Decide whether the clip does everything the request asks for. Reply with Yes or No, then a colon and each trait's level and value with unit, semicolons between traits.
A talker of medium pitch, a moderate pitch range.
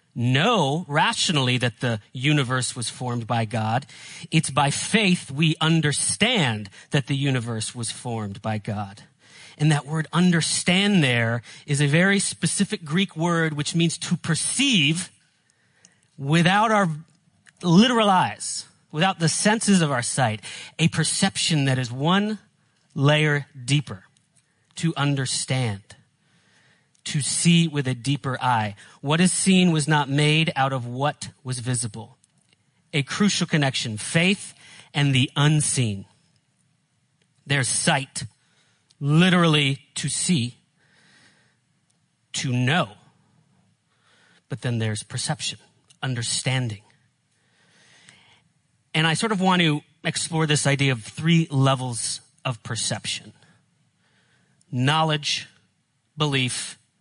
Yes: medium, 145 Hz; average, 4.3 semitones